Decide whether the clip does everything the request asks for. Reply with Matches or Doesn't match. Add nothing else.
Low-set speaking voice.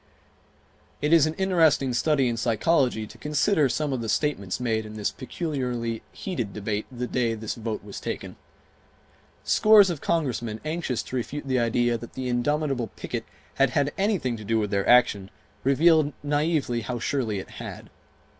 Matches